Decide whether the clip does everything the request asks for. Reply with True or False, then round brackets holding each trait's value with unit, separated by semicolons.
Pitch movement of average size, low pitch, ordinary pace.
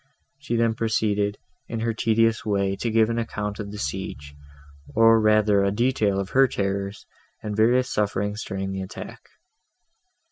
False (2.3 semitones; 105 Hz; 155 wpm)